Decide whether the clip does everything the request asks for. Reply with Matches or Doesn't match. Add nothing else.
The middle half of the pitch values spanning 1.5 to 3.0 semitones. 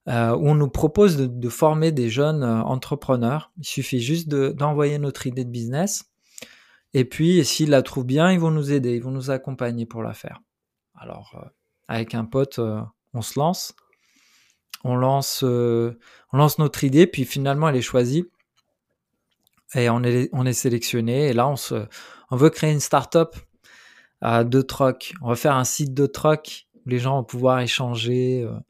Doesn't match